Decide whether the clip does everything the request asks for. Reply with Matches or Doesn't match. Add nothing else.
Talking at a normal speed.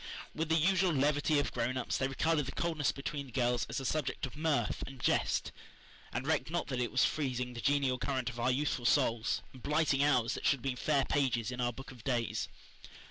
Doesn't match